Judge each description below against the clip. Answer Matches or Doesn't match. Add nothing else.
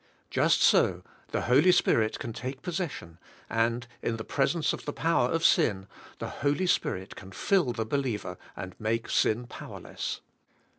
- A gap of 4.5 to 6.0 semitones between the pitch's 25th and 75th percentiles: Matches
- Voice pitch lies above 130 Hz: Doesn't match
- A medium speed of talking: Matches